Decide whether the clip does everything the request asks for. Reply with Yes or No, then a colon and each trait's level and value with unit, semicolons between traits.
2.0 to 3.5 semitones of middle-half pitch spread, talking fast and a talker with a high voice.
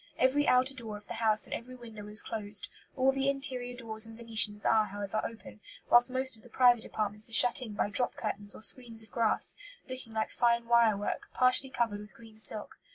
Yes: average, 2.8 semitones; fast, 215 wpm; high, 230 Hz